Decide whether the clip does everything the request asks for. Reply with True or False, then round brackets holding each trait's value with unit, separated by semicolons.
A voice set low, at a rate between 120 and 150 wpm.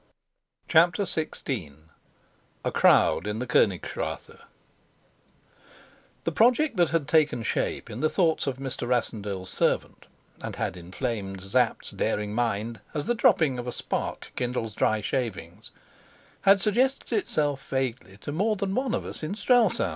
True (130 Hz; 140 wpm)